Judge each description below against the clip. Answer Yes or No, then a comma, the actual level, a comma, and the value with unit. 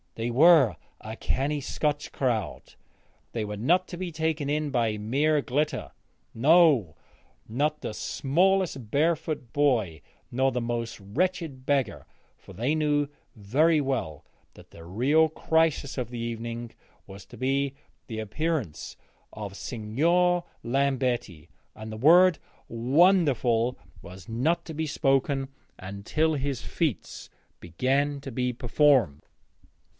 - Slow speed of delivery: Yes, slow, 125 wpm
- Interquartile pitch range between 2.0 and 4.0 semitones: No, average, 5.1 semitones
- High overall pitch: No, low, 135 Hz